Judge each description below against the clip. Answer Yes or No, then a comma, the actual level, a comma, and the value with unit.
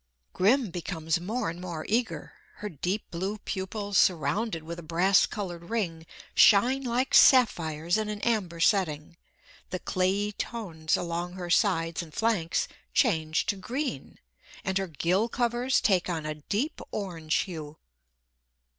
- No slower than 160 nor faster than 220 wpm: No, average, 140 wpm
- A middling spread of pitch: Yes, average, 4.4 semitones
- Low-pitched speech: No, medium, 185 Hz